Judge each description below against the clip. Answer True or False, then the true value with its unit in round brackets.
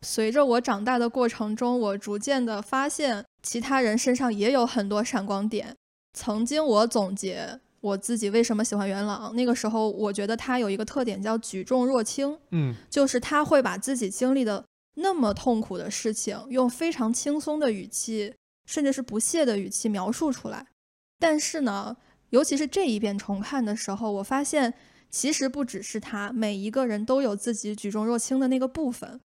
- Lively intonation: False (3.9 semitones)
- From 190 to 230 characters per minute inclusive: False (285 characters per minute)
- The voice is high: True (235 Hz)